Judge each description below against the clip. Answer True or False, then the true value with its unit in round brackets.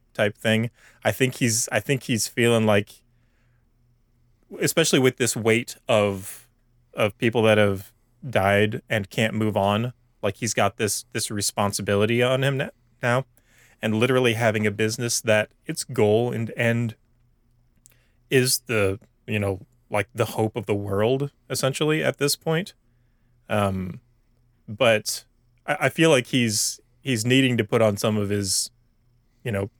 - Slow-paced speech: False (150 wpm)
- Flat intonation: True (2.1 semitones)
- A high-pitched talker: False (120 Hz)